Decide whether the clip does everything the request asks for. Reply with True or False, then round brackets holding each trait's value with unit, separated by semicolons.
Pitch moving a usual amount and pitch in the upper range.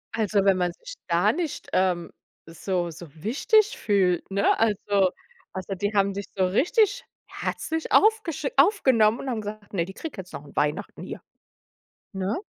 False (6.6 semitones; 205 Hz)